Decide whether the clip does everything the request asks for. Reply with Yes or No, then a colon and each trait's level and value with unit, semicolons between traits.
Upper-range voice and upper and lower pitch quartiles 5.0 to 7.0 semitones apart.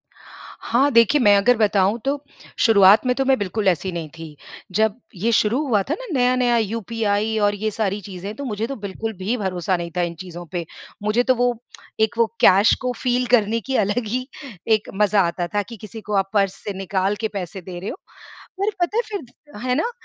No: high, 215 Hz; average, 4.1 semitones